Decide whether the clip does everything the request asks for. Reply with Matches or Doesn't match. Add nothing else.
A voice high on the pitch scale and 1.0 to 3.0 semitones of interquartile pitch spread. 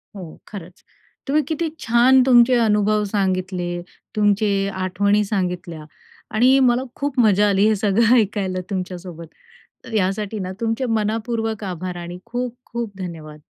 Doesn't match